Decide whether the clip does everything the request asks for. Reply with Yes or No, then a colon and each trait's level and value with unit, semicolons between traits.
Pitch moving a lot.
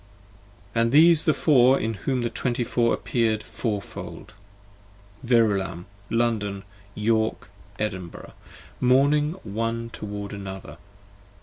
No: average, 3.3 semitones